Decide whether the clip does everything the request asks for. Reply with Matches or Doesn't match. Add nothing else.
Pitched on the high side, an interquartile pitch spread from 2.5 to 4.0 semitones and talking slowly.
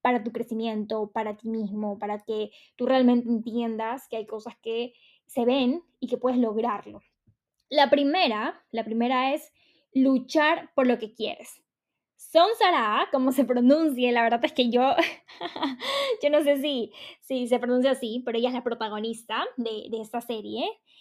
Doesn't match